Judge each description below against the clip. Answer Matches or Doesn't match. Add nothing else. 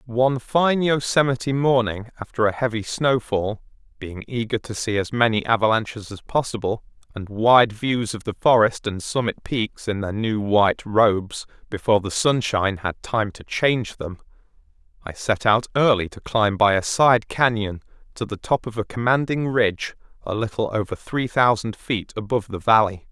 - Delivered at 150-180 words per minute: Matches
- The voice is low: Matches